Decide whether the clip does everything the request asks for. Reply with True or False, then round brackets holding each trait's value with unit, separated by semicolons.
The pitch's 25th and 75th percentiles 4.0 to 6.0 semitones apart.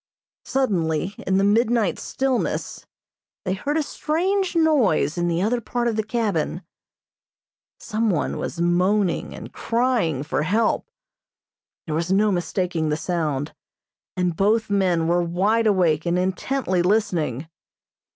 True (5.1 semitones)